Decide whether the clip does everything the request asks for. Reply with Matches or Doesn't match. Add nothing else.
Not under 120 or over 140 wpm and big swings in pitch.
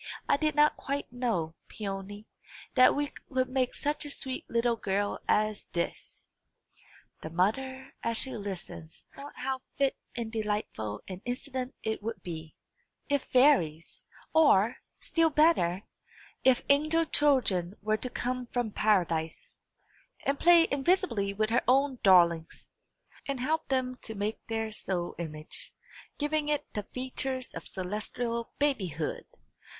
Matches